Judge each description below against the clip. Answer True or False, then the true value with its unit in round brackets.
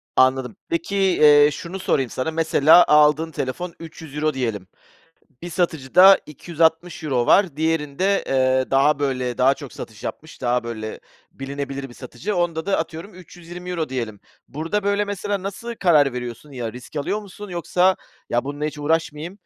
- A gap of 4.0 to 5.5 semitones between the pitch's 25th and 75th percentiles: True (4.9 semitones)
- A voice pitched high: False (150 Hz)